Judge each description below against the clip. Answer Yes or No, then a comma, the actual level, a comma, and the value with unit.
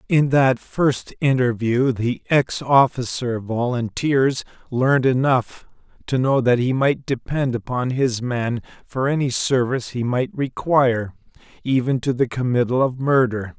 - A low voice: Yes, low, 125 Hz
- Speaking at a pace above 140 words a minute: No, slow, 135 wpm